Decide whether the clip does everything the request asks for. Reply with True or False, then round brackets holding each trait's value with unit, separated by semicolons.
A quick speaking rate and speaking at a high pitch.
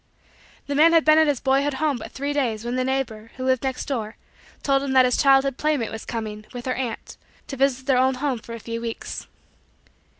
True (225 wpm; 260 Hz)